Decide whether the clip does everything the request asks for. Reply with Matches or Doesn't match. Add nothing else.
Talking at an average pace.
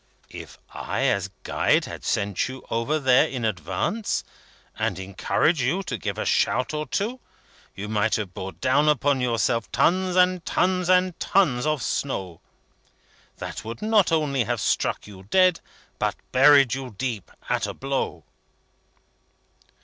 Matches